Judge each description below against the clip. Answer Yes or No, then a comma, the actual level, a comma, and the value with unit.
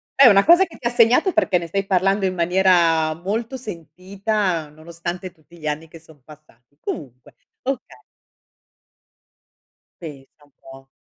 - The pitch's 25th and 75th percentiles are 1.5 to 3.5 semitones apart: No, average, 4.3 semitones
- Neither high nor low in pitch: Yes, medium, 175 Hz